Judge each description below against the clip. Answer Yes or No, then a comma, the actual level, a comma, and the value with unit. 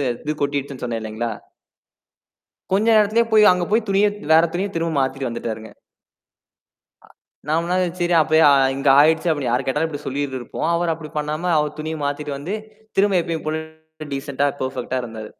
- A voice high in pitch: No, medium, 150 Hz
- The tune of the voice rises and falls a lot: No, average, 4.3 semitones